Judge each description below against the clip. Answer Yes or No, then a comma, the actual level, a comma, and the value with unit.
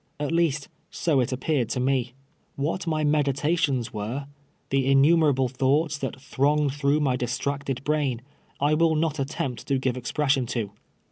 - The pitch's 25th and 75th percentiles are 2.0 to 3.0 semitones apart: Yes, narrow, 2.6 semitones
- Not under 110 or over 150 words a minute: No, average, 175 wpm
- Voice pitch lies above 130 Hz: Yes, medium, 140 Hz